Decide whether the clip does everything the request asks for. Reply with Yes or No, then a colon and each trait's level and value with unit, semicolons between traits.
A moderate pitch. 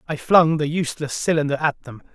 Yes: medium, 150 Hz